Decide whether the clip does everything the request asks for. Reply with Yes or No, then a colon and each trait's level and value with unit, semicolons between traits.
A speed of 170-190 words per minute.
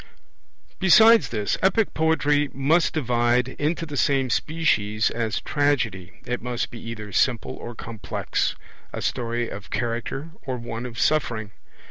No: slow, 135 wpm